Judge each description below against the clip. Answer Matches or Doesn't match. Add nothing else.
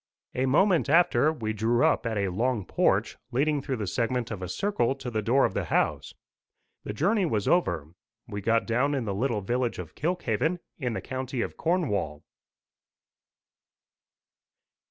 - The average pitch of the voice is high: Doesn't match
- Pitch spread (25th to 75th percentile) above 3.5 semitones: Matches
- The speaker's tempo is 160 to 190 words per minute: Matches